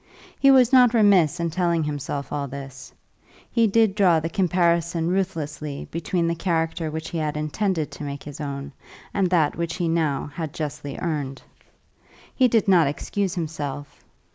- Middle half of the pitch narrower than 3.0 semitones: No, average, 3.8 semitones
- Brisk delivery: No, average, 165 wpm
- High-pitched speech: No, medium, 165 Hz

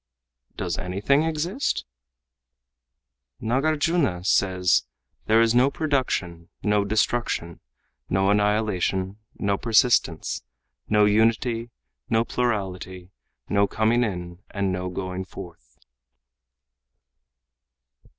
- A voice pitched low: Yes, low, 105 Hz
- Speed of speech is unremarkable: No, slow, 85 wpm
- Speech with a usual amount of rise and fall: Yes, average, 4.5 semitones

